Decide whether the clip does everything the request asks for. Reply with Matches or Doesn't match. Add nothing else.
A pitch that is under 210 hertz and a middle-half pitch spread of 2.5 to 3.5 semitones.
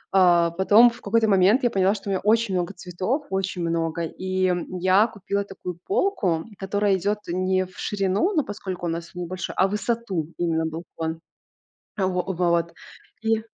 Matches